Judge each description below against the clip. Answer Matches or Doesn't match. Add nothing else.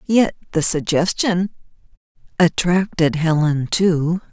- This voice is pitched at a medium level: Matches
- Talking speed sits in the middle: Doesn't match